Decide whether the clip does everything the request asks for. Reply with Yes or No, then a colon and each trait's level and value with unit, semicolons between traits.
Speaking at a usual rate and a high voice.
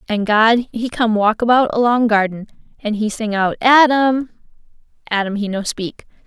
Yes: average, 165 wpm; high, 225 Hz